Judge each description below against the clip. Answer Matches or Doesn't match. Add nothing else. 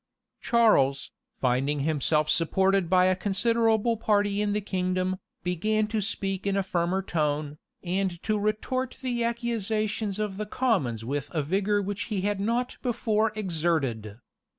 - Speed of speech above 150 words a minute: Doesn't match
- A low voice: Doesn't match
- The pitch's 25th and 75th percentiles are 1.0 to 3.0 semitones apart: Doesn't match